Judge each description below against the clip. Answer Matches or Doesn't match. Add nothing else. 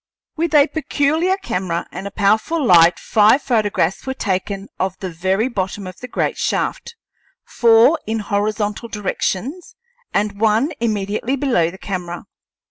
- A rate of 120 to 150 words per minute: Matches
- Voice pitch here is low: Doesn't match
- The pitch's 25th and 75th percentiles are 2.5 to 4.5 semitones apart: Doesn't match